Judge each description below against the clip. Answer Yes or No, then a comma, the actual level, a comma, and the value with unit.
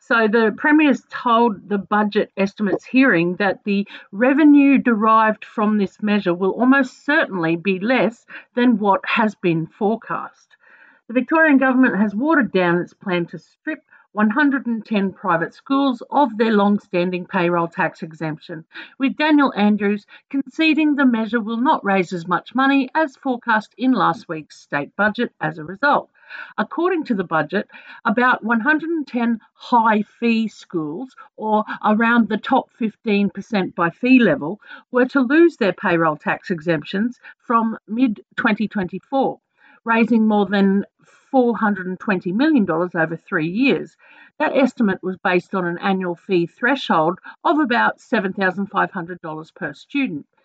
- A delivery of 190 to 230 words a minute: No, average, 140 wpm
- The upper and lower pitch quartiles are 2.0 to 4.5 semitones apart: No, wide, 5.6 semitones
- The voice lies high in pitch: Yes, high, 215 Hz